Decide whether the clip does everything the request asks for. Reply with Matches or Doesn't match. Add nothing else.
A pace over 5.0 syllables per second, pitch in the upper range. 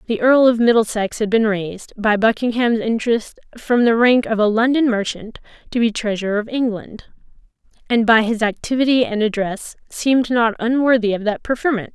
Matches